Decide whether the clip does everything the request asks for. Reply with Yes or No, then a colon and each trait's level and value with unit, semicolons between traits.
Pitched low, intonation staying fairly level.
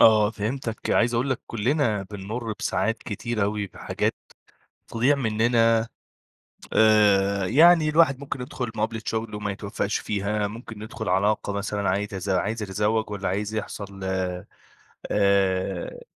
Yes: low, 105 Hz; narrow, 2.3 semitones